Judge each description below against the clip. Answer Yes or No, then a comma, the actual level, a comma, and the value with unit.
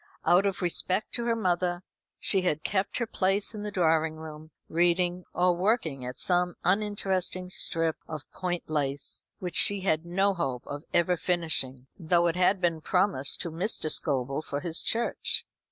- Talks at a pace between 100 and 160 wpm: No, average, 170 wpm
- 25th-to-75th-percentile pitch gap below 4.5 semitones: Yes, average, 3.1 semitones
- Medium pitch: Yes, medium, 175 Hz